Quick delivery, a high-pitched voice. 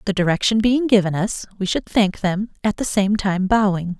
Yes: fast, 210 wpm; high, 200 Hz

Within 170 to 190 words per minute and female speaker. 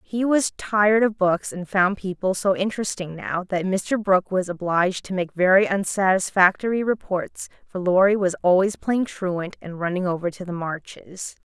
Yes: average, 175 wpm; female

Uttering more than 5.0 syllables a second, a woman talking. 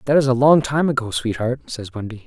No: 5.8 syllables/s; male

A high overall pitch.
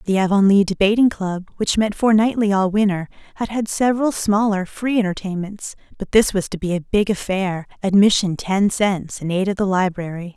Yes: high, 200 Hz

